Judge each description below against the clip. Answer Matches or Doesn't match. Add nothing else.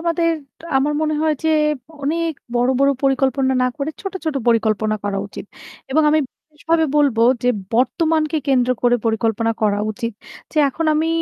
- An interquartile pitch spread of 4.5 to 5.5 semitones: Matches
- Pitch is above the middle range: Matches